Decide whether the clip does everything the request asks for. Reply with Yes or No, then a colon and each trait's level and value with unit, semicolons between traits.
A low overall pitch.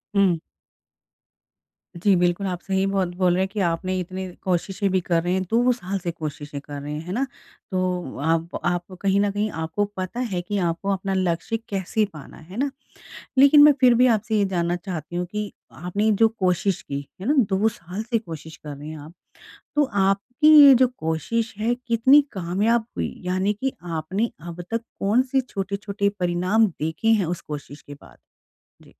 No: high, 190 Hz